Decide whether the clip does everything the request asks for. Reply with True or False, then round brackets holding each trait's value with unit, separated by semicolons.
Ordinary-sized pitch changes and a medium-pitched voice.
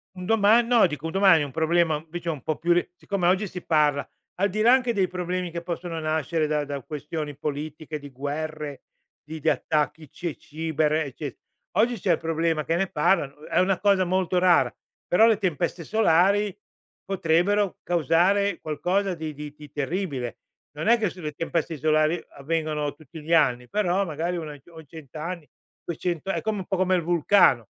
True (3.4 semitones; 165 Hz)